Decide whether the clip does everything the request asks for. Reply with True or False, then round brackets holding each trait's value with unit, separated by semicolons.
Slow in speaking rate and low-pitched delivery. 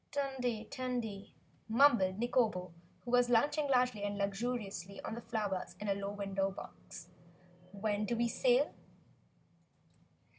False (125 wpm; 220 Hz)